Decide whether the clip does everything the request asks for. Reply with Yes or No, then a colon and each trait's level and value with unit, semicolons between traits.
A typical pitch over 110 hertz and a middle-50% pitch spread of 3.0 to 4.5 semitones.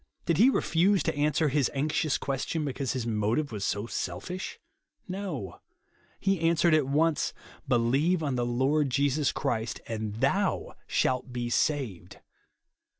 No: medium, 140 Hz; average, 4.9 semitones